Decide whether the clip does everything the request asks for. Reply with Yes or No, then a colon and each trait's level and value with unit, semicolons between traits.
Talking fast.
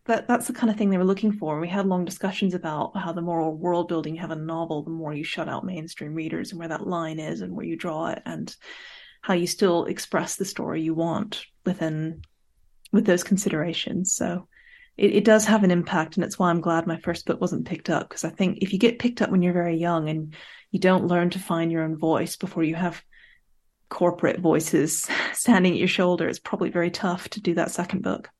Yes: fast, 240 wpm